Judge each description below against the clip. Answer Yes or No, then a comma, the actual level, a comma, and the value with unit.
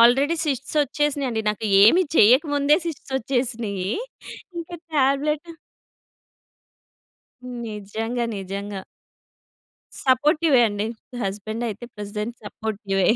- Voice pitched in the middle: No, high, 240 Hz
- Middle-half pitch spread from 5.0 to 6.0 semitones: Yes, average, 5.3 semitones